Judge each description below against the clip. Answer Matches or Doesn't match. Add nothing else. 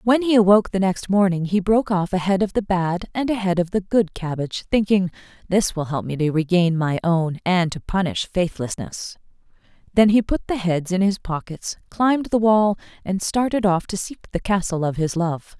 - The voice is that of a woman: Matches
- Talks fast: Matches